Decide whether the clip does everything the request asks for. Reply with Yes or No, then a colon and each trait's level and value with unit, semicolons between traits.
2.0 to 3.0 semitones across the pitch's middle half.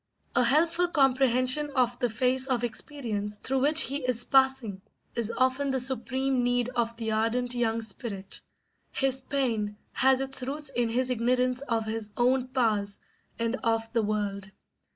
Yes: average, 2.7 semitones